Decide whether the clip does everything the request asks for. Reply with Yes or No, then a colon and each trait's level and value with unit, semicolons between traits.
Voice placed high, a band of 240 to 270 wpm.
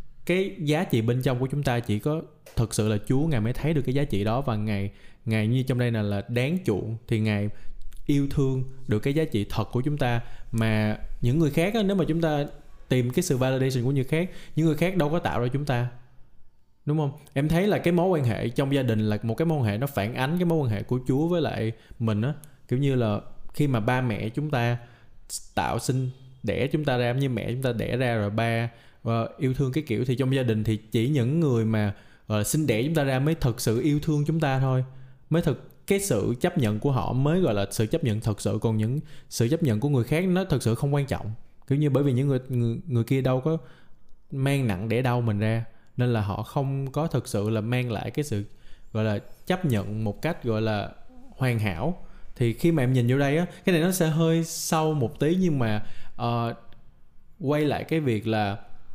No: low, 125 Hz; average, 245 wpm